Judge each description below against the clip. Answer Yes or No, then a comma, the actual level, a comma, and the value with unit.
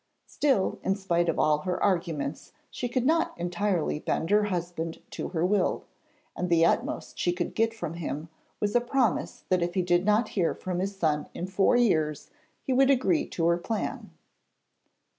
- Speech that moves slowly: No, average, 180 wpm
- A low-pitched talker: No, medium, 180 Hz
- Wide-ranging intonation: No, average, 3.8 semitones